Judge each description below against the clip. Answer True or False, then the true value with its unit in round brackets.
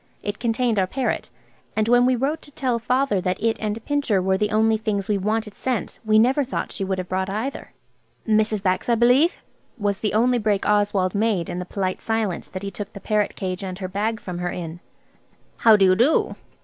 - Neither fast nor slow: False (215 wpm)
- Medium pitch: False (215 Hz)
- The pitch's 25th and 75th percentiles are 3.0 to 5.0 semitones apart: True (3.4 semitones)